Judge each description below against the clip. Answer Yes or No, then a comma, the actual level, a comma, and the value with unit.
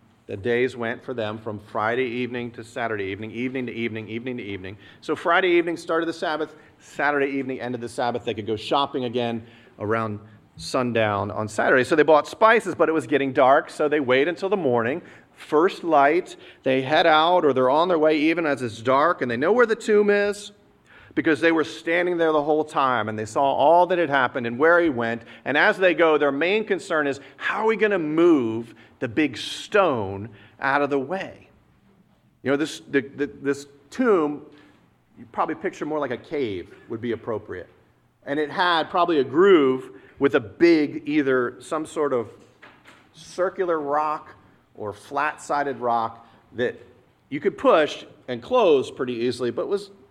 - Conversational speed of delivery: Yes, average, 190 wpm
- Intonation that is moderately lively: No, wide, 6.0 semitones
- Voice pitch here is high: No, medium, 140 Hz